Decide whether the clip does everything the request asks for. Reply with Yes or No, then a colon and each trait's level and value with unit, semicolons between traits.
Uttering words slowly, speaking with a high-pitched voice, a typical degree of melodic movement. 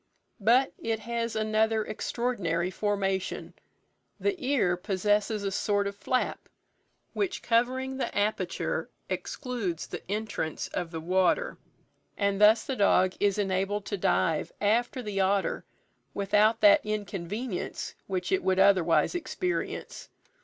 Yes: slow, 125 wpm; high, 205 Hz; average, 3.4 semitones